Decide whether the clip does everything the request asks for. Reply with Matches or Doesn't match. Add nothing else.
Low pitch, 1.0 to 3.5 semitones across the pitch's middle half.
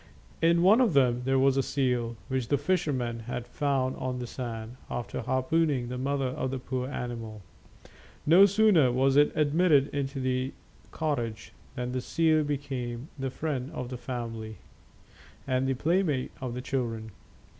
Matches